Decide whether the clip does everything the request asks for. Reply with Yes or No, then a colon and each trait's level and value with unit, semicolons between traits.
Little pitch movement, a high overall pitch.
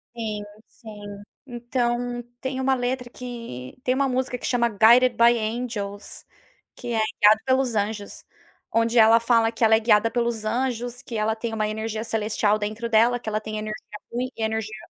Yes: narrow, 2.2 semitones; high, 230 Hz